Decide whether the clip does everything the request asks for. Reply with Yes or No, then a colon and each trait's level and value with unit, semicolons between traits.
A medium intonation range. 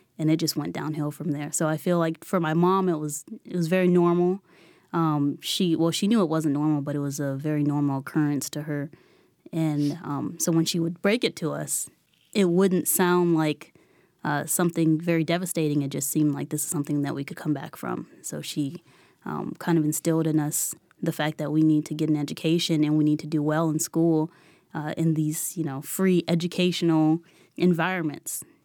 No: narrow, 2.2 semitones